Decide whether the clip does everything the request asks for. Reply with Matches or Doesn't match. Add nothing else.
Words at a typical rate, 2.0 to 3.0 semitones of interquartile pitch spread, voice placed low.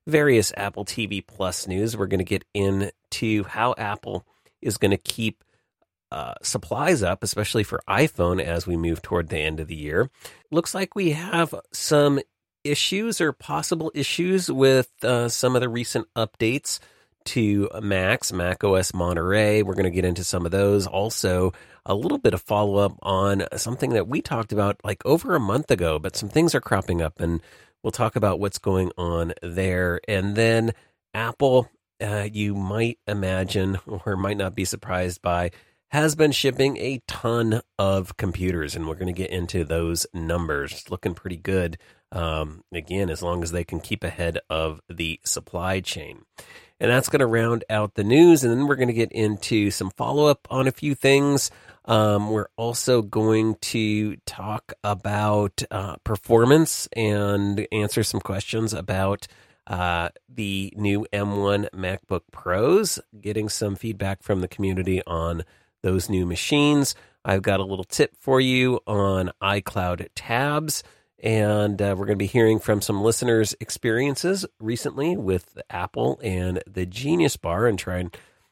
Doesn't match